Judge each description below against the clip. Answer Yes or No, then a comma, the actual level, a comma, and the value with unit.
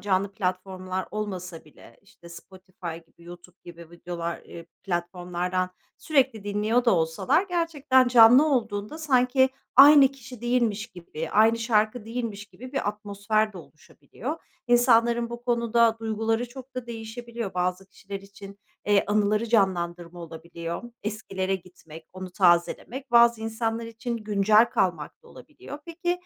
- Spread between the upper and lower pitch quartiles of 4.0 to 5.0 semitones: Yes, average, 4.6 semitones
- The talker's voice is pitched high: Yes, high, 210 Hz